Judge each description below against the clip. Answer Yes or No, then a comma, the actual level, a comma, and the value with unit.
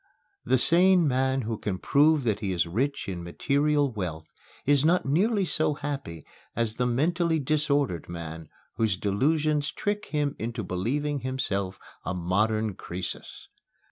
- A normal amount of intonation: No, wide, 7.3 semitones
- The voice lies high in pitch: No, low, 130 Hz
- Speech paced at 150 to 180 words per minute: No, average, 140 wpm